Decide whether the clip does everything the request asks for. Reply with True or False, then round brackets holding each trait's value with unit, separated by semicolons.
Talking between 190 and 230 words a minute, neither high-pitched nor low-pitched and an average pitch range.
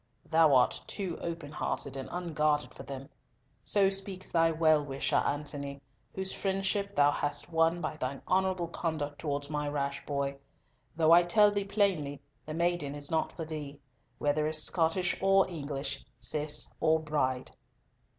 False (155 wpm; 155 Hz; 3.4 semitones)